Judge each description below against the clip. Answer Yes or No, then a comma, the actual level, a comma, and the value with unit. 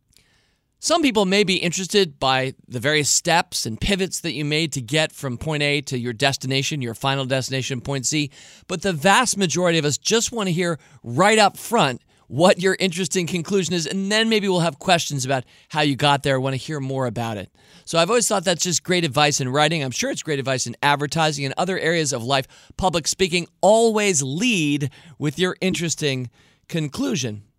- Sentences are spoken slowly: No, average, 200 wpm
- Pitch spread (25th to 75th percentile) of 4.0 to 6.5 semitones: Yes, wide, 5.4 semitones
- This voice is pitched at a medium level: Yes, medium, 155 Hz